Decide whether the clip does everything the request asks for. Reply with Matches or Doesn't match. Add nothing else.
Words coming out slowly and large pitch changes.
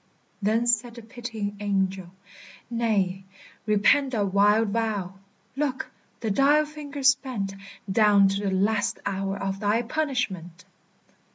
Doesn't match